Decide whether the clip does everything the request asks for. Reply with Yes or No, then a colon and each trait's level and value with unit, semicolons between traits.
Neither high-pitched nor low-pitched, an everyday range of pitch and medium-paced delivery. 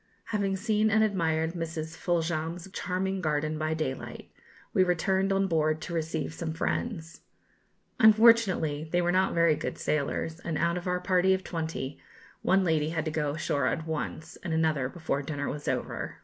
Yes: medium, 165 Hz; average, 3.1 semitones; average, 170 wpm